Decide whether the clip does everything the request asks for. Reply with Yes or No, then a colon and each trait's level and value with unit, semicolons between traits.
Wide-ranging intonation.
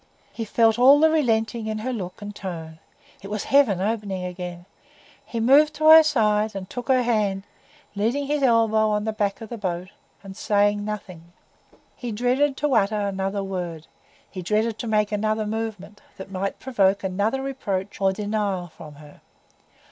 No: average, 3.2 semitones